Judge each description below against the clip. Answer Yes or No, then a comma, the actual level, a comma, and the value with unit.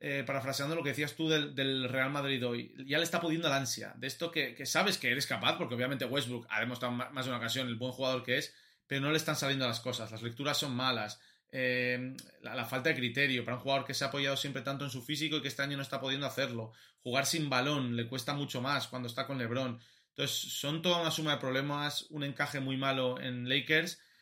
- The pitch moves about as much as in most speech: No, narrow, 2.2 semitones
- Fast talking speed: Yes, fast, 250 wpm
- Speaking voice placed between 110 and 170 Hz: Yes, low, 135 Hz